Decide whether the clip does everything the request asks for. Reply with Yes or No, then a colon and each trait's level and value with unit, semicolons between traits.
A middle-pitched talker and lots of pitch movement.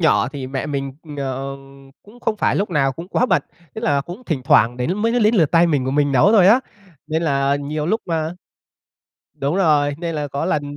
No: medium, 150 Hz; average, 4.5 semitones